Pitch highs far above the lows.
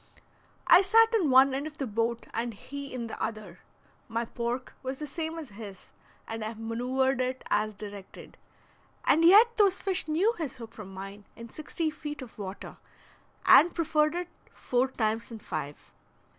Yes: wide, 5.9 semitones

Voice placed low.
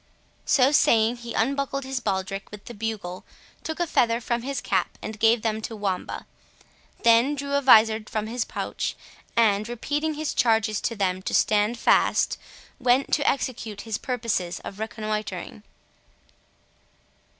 No: high, 225 Hz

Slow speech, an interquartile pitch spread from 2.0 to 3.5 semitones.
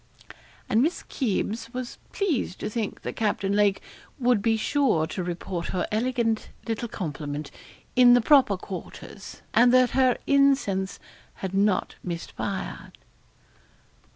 No: slow, 130 wpm; average, 4.7 semitones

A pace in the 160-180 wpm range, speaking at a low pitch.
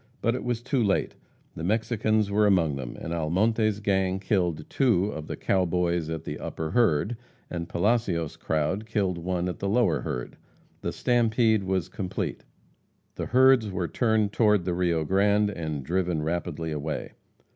Yes: average, 165 wpm; very low, 95 Hz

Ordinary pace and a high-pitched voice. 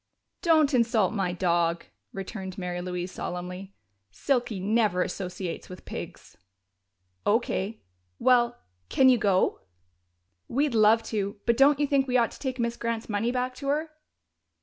Yes: average, 145 wpm; high, 220 Hz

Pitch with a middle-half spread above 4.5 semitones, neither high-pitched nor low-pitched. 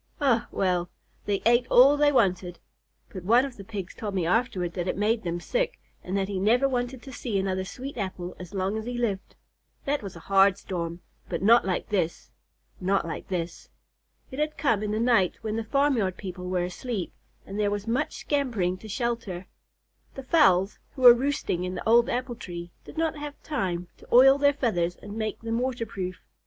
No: average, 5.1 semitones; high, 210 Hz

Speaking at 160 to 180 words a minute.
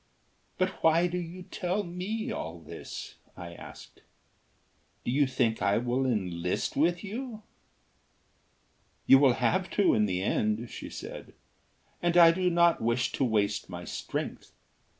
No: average, 145 wpm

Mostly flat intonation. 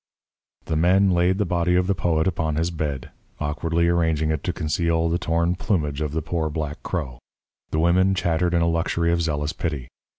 Yes: narrow, 2.0 semitones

